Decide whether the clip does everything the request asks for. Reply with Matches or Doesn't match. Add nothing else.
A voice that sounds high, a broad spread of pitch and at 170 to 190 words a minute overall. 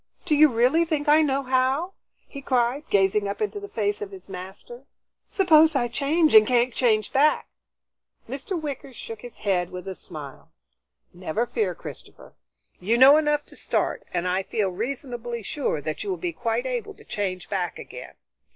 Matches